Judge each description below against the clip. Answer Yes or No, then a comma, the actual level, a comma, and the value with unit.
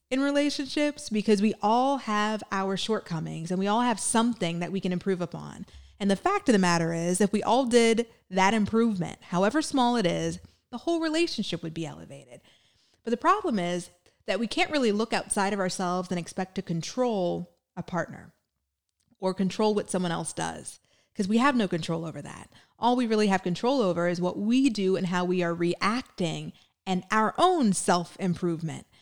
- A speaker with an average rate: Yes, average, 190 wpm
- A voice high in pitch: Yes, high, 195 Hz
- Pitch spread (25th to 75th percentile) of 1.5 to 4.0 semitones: No, average, 5.1 semitones